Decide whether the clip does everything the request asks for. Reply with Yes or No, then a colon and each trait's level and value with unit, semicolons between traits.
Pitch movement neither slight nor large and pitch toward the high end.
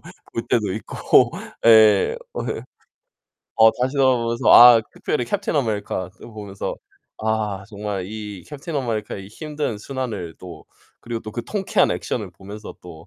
No: average, 3.4 semitones; low, 110 Hz